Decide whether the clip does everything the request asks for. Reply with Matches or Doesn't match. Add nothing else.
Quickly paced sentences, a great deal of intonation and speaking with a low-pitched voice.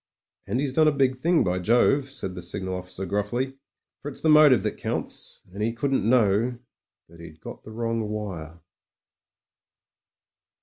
Doesn't match